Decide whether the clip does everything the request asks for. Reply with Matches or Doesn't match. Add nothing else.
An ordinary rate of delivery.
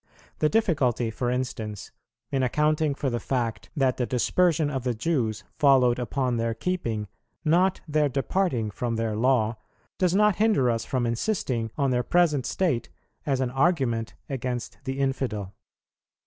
Matches